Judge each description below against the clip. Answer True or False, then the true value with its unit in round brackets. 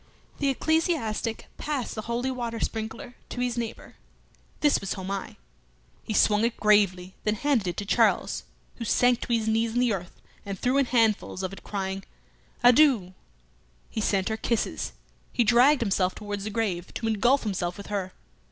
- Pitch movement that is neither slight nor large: True (3.6 semitones)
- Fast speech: False (170 wpm)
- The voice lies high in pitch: True (220 Hz)